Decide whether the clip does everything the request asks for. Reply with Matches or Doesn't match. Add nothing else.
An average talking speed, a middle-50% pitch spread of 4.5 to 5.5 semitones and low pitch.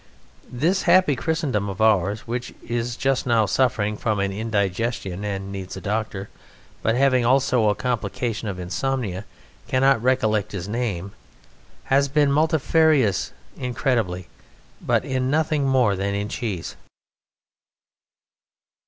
Doesn't match